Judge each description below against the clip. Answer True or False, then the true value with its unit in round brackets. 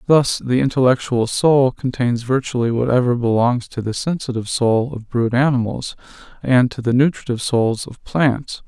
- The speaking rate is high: False (150 wpm)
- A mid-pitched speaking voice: False (125 Hz)